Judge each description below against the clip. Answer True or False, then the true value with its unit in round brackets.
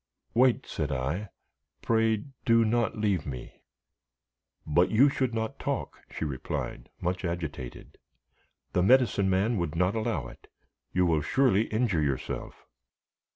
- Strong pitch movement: True (6.0 semitones)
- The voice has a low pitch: True (95 Hz)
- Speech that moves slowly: True (130 wpm)